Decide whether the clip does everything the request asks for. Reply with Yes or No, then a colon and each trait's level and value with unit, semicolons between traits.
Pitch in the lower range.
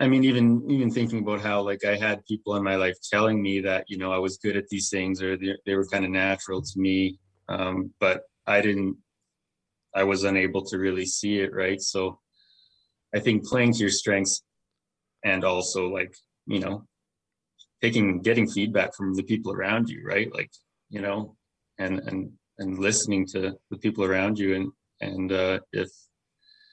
Yes: low, 100 Hz